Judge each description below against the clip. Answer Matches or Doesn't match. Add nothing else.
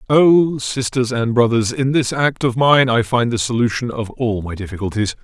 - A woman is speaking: Doesn't match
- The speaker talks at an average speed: Matches